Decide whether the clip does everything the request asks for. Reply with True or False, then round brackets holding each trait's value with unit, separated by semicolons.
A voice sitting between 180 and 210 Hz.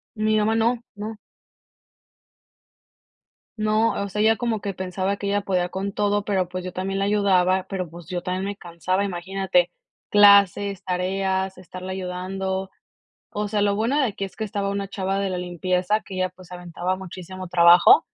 True (190 Hz)